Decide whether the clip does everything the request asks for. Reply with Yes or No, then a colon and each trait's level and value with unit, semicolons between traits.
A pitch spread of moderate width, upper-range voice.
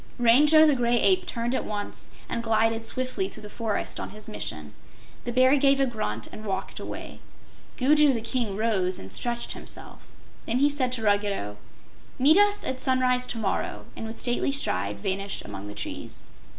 Yes: average, 4.1 semitones; high, 235 Hz